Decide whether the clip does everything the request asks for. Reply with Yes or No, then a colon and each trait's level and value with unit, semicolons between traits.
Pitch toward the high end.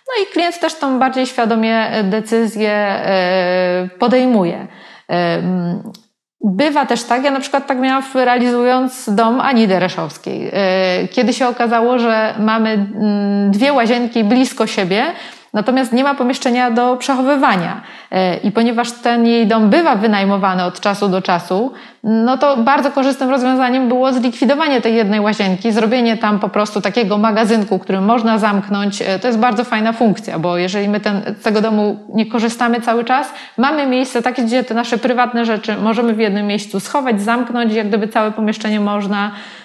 Yes: high, 230 Hz